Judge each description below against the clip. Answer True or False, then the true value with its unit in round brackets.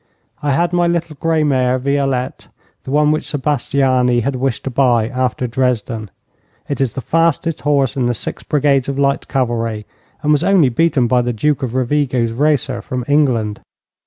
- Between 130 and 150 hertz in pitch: True (135 Hz)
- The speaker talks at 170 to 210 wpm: True (175 wpm)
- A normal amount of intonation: True (3.0 semitones)